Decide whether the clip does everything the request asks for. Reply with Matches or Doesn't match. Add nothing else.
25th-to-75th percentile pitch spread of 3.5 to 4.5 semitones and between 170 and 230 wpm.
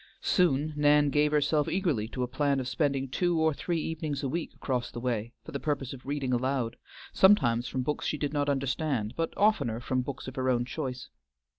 Doesn't match